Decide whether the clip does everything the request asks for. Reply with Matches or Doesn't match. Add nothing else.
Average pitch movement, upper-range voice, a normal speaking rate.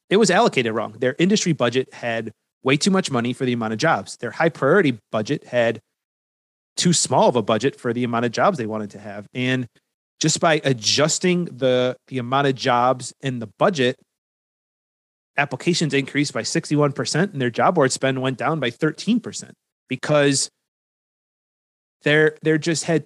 Doesn't match